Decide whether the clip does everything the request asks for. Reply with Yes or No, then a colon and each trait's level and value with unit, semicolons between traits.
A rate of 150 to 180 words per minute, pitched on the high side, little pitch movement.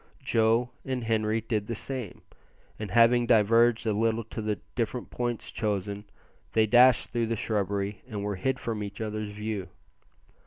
No: average, 160 wpm; low, 110 Hz; narrow, 2.0 semitones